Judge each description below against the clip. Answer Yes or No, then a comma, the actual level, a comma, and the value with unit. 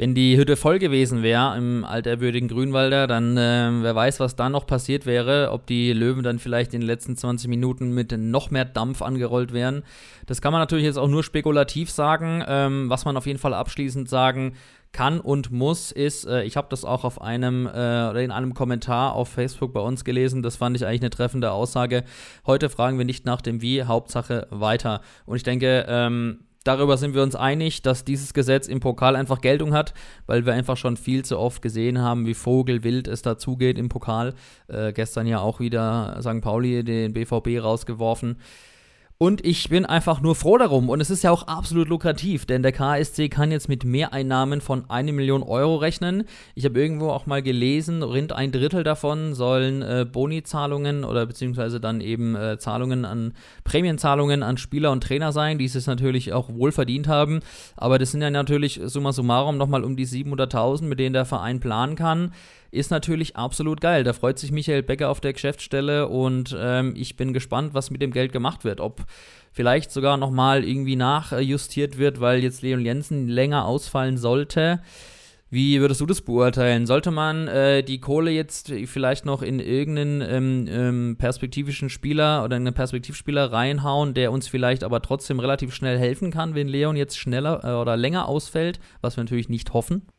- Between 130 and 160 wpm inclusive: No, fast, 190 wpm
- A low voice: Yes, low, 130 Hz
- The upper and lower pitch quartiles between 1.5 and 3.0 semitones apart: Yes, narrow, 2.6 semitones